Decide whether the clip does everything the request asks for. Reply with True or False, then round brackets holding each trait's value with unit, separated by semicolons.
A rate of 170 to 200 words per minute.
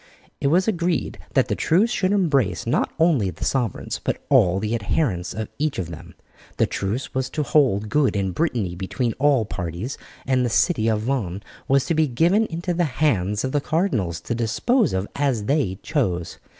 True (190 wpm)